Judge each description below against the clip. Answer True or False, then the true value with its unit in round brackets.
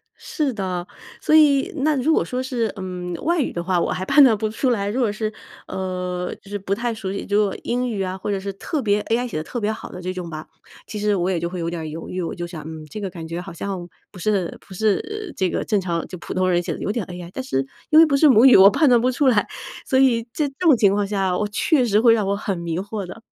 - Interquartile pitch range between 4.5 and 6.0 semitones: True (5.1 semitones)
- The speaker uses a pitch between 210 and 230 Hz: False (200 Hz)